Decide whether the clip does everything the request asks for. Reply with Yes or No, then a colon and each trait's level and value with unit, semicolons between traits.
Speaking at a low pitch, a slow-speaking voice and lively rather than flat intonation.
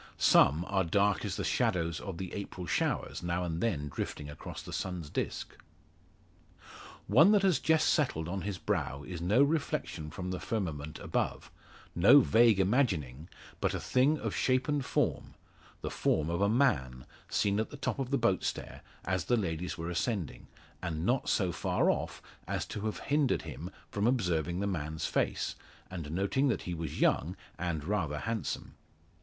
No: very low, 95 Hz; average, 175 wpm; wide, 6.2 semitones